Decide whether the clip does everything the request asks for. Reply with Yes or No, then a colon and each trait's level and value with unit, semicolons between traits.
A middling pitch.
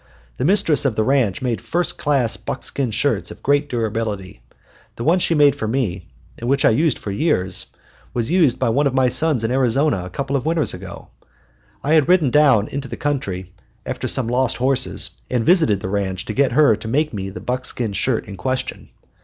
No: low, 130 Hz